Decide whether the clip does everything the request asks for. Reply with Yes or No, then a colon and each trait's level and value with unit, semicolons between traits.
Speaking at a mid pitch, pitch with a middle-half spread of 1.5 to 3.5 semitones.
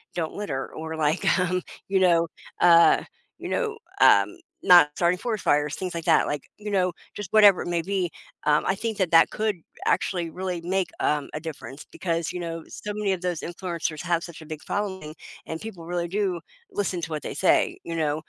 Yes: medium, 175 Hz; average, 2.8 semitones